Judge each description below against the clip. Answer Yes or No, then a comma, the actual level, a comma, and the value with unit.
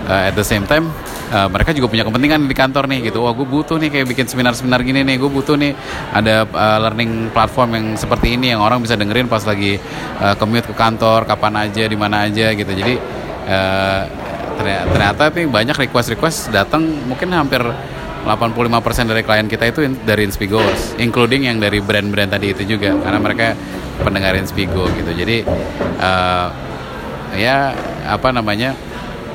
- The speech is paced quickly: Yes, fast, 170 wpm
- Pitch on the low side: Yes, low, 110 Hz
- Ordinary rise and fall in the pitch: Yes, average, 3.8 semitones